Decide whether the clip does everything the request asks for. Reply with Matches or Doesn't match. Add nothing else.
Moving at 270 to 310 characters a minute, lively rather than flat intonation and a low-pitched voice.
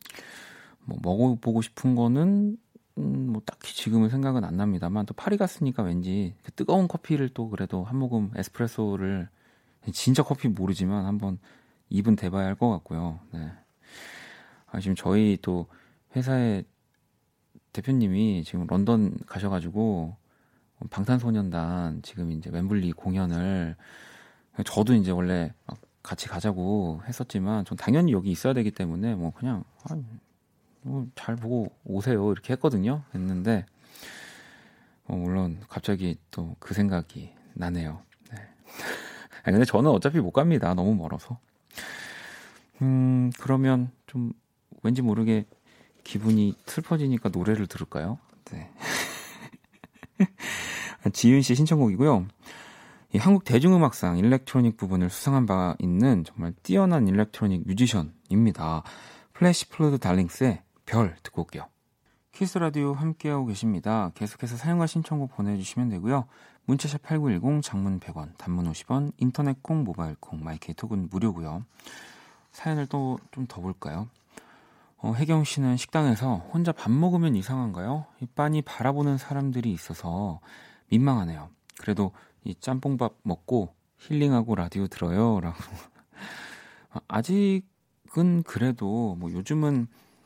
Matches